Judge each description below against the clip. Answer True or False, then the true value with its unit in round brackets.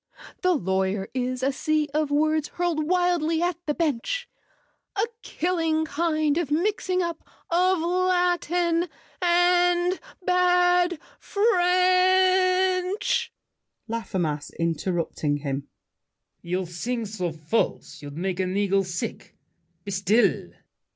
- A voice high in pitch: True (320 Hz)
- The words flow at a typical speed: False (105 wpm)